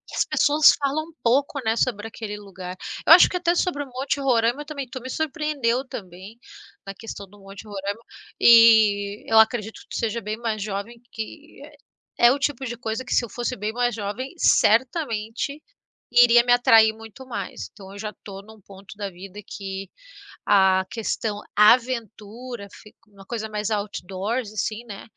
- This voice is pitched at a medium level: No, high, 225 Hz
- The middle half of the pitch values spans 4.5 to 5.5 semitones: No, average, 3.7 semitones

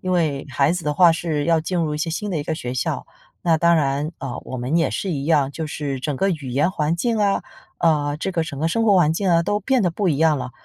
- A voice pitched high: No, medium, 160 Hz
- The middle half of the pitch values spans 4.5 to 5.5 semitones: No, average, 3.3 semitones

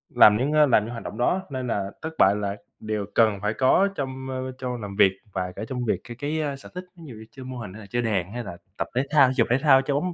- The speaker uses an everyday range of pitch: Yes, average, 4.3 semitones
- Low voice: Yes, low, 125 Hz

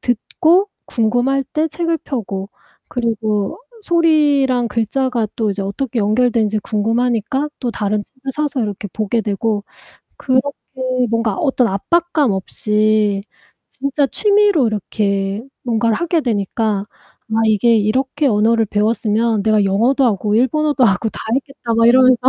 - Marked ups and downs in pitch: No, average, 4.2 semitones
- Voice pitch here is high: Yes, high, 230 Hz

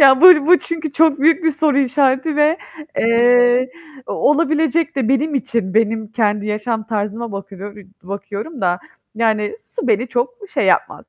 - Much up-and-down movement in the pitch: Yes, wide, 6.0 semitones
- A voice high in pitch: Yes, high, 245 Hz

